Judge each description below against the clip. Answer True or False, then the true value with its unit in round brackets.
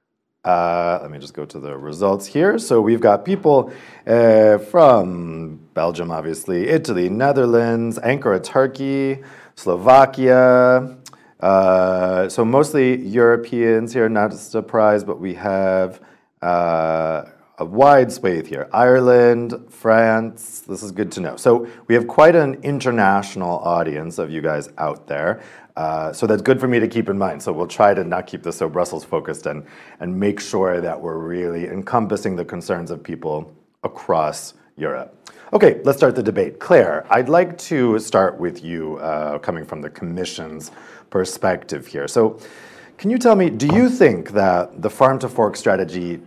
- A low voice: True (110 Hz)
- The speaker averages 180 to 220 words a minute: False (160 wpm)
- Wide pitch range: True (6.3 semitones)